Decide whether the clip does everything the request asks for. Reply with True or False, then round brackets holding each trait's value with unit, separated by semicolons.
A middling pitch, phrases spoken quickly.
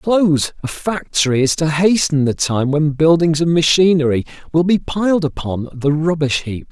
False (155 Hz; 180 wpm)